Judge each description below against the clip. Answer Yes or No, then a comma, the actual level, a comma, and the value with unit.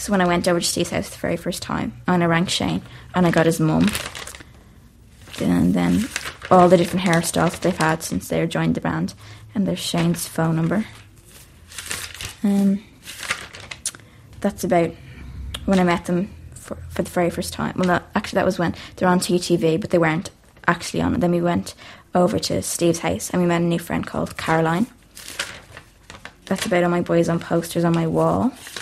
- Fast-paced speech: No, average, 195 wpm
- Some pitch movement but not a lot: No, narrow, 2.2 semitones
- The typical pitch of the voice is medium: Yes, medium, 170 Hz